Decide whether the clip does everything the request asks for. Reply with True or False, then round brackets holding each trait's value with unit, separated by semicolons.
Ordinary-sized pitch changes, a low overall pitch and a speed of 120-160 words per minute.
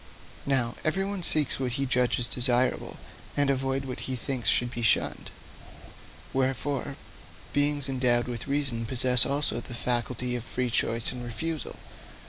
False (2.3 semitones; 130 Hz; 140 wpm)